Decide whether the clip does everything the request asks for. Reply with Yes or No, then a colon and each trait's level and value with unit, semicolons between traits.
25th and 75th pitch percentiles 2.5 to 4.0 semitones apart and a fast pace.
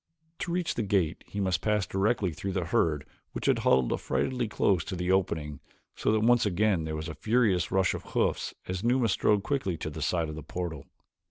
No: average, 4.8 semitones; fast, 210 wpm